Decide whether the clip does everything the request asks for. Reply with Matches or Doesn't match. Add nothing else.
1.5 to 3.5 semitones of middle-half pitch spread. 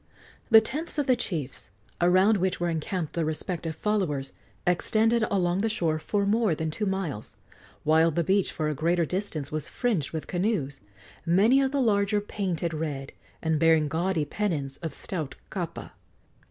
Doesn't match